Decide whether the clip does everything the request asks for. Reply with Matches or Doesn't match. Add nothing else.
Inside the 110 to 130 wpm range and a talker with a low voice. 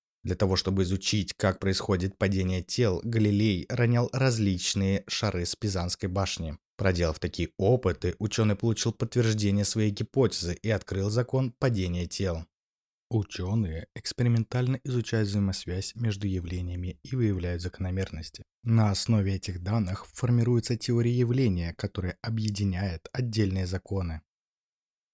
Matches